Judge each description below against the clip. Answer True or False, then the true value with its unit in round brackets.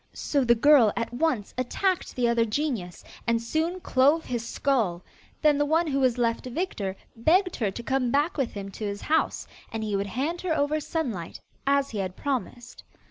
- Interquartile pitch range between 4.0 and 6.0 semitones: True (5.0 semitones)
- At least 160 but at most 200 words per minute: True (190 wpm)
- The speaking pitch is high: True (255 Hz)